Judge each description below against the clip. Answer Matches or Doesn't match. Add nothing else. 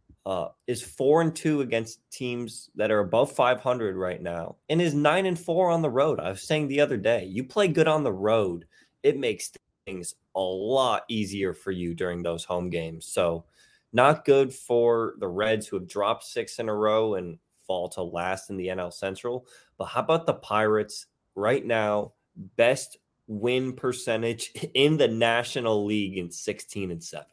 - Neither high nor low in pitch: Doesn't match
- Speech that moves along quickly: Doesn't match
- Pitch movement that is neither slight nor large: Doesn't match